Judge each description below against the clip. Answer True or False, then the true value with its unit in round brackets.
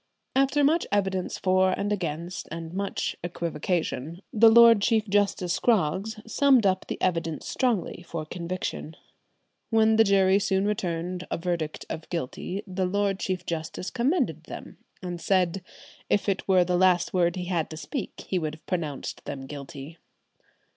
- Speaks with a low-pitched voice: False (185 Hz)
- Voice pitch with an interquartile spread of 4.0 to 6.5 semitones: False (3.2 semitones)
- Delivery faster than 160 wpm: False (155 wpm)